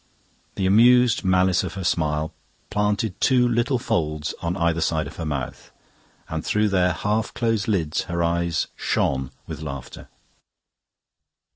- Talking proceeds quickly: No, average, 140 wpm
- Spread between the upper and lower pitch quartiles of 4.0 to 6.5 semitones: Yes, average, 5.0 semitones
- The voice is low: Yes, very low, 90 Hz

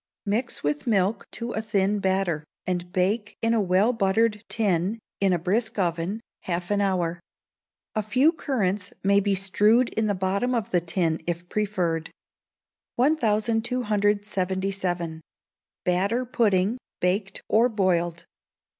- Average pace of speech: No, slow, 130 wpm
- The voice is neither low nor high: No, high, 200 Hz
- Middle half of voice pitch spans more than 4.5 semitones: No, average, 3.5 semitones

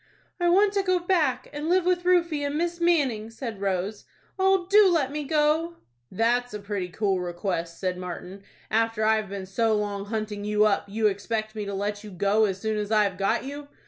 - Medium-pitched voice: No, high, 220 Hz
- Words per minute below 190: No, fast, 205 wpm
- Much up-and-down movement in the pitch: Yes, wide, 7.1 semitones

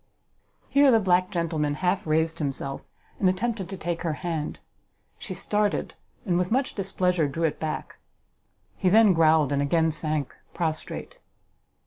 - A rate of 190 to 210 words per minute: No, average, 145 wpm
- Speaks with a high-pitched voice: No, medium, 170 Hz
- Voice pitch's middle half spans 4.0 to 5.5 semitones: No, average, 3.6 semitones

